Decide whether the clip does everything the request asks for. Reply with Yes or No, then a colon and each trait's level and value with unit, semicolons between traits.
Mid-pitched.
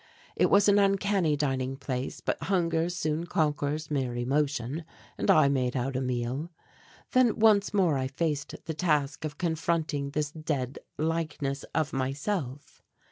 Yes: medium, 150 Hz